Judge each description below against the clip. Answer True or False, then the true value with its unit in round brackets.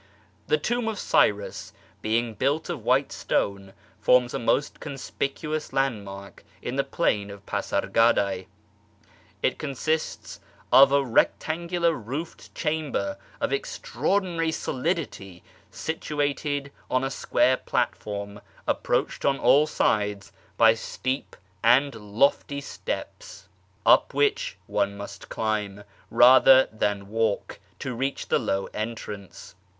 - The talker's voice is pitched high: False (130 Hz)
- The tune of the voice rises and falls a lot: True (6.2 semitones)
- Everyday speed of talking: False (115 wpm)